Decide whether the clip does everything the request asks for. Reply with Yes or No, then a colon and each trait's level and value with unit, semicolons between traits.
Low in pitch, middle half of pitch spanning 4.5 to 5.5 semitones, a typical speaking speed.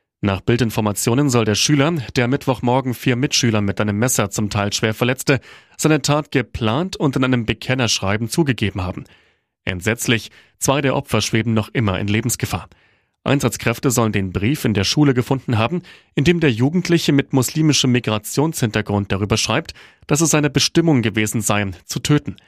Yes: low, 120 Hz; average, 4.8 semitones; average, 160 wpm